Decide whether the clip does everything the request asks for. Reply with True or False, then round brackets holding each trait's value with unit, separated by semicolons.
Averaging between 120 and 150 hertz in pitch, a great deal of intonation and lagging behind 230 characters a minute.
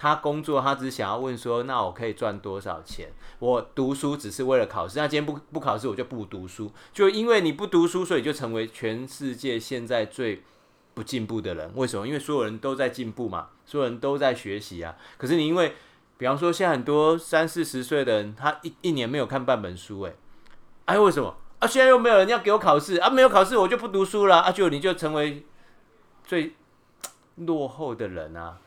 False (140 Hz; 5.8 semitones; 320 characters per minute)